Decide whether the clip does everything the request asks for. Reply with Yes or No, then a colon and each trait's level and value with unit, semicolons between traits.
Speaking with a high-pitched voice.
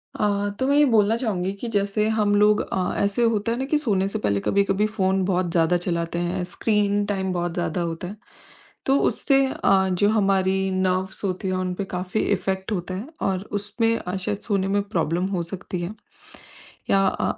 Yes: high, 195 Hz